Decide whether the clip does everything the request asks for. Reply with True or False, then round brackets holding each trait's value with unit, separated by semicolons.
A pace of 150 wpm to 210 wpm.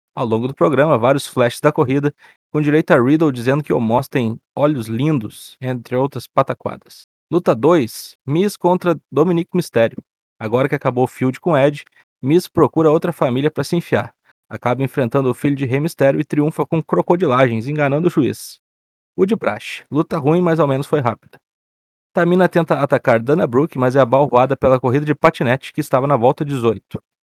True (180 wpm)